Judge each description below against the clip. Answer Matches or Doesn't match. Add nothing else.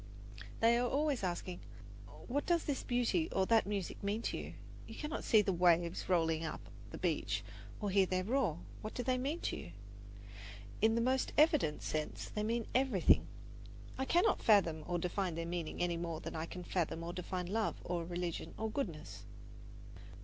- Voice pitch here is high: Matches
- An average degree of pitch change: Doesn't match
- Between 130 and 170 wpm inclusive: Doesn't match